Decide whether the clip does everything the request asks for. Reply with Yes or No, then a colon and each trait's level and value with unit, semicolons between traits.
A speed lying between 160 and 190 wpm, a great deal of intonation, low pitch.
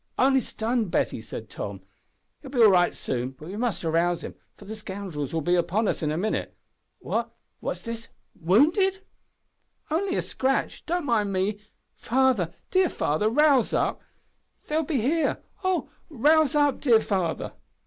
No: average, 165 wpm; wide, 8.4 semitones; high, 220 Hz